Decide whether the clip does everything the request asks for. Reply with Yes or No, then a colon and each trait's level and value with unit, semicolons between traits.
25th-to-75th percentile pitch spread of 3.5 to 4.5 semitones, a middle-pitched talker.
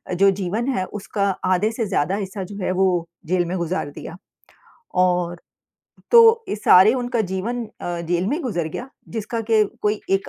No: average, 4.0 semitones; high, 195 Hz